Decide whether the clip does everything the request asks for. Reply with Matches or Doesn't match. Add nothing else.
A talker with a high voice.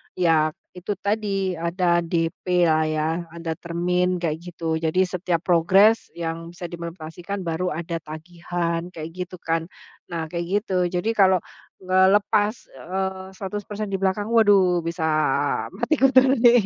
Doesn't match